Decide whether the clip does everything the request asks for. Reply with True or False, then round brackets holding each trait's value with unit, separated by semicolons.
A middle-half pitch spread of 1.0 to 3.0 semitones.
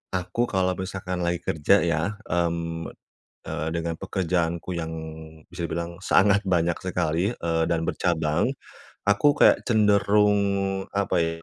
True (2.7 semitones)